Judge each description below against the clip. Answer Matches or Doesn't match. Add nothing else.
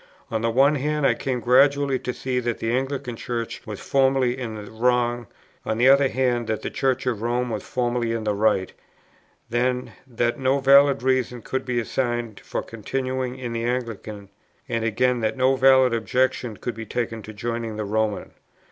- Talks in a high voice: Doesn't match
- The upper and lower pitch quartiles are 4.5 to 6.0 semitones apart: Doesn't match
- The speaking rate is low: Doesn't match